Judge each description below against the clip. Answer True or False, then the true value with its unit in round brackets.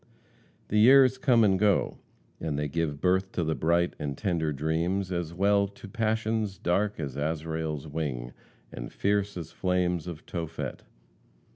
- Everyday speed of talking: True (150 wpm)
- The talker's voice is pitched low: True (90 Hz)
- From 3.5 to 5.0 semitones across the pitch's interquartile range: True (4.2 semitones)